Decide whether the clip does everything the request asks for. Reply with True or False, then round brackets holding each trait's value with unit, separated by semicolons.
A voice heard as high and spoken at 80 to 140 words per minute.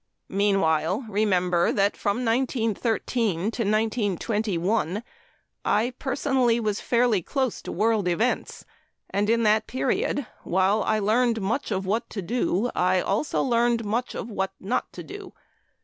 True (215 Hz; 135 wpm)